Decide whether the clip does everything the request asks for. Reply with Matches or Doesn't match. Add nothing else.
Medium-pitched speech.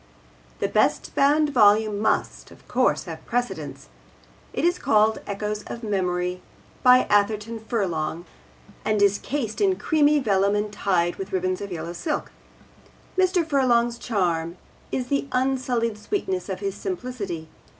Doesn't match